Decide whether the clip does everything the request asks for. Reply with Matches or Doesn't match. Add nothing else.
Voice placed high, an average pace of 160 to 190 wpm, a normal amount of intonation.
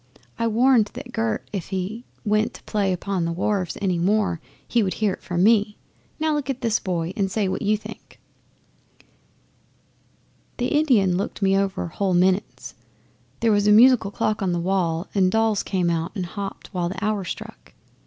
Matches